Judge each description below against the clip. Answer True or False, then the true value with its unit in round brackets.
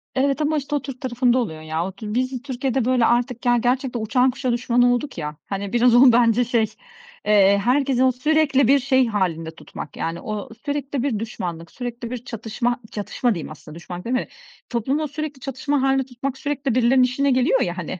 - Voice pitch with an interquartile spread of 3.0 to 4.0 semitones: True (3.4 semitones)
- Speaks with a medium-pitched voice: False (245 Hz)